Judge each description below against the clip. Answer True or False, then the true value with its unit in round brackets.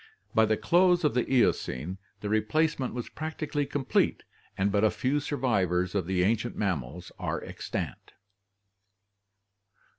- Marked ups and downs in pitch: True (7.2 semitones)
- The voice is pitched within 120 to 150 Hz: False (110 Hz)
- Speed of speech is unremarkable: False (125 wpm)